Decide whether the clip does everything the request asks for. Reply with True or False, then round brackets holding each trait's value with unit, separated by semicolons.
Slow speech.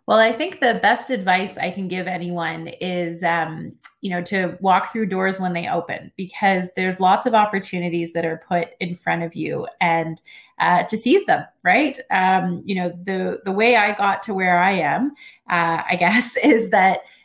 False (195 wpm)